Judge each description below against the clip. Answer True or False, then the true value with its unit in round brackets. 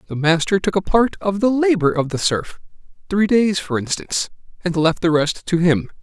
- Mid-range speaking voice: True (180 Hz)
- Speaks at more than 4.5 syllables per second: True (5.1 syllables/s)